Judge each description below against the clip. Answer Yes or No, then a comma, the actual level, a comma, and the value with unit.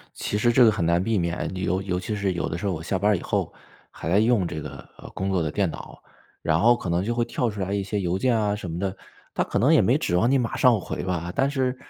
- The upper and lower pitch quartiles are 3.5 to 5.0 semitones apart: Yes, average, 4.3 semitones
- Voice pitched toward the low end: Yes, very low, 95 Hz